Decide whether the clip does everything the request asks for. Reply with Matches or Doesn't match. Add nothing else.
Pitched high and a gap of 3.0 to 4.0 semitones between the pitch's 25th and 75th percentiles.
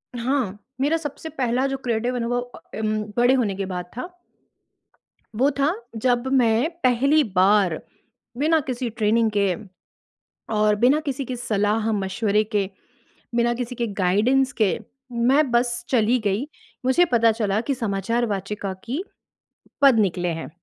Matches